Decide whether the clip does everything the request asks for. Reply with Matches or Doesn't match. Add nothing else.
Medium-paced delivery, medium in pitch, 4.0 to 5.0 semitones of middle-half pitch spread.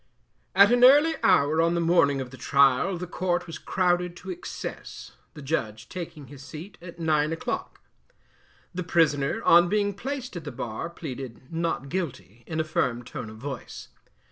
Matches